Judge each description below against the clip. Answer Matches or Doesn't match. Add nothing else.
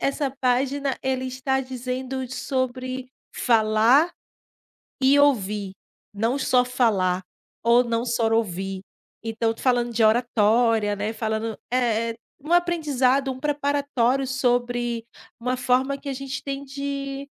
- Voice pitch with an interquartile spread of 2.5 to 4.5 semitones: Matches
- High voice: Matches